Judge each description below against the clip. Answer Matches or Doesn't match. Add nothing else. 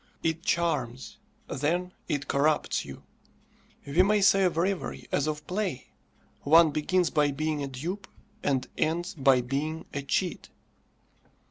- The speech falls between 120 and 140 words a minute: Matches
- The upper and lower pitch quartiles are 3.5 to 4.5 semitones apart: Matches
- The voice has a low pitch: Doesn't match